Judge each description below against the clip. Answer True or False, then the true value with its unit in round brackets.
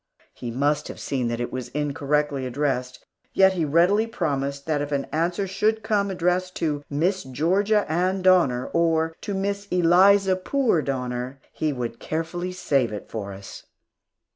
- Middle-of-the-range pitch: True (160 Hz)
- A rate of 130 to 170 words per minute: True (160 wpm)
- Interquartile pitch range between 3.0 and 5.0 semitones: False (5.4 semitones)